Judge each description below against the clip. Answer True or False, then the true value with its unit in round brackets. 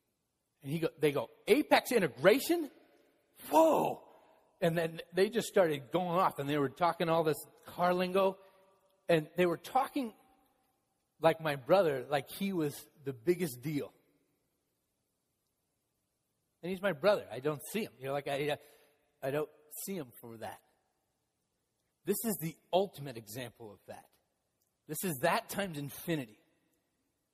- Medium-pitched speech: True (170 Hz)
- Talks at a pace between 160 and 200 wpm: False (145 wpm)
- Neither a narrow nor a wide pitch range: True (5.0 semitones)